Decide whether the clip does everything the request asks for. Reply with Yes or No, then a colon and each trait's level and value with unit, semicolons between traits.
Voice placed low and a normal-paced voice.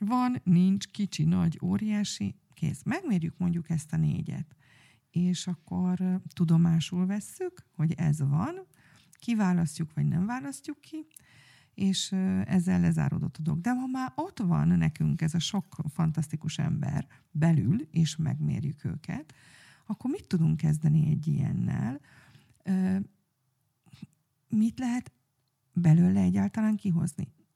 No: medium, 170 Hz; average, 115 wpm